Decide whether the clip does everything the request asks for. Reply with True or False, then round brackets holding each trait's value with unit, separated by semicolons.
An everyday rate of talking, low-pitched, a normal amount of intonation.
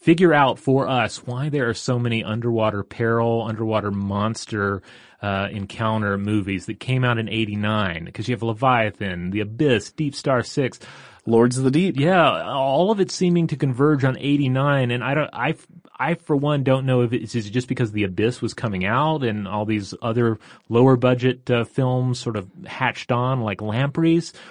True (185 wpm; 120 Hz; 4.0 semitones)